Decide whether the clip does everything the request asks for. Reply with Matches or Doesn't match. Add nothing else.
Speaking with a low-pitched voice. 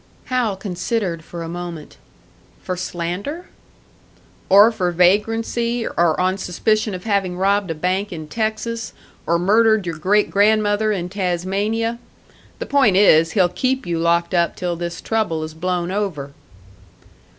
Doesn't match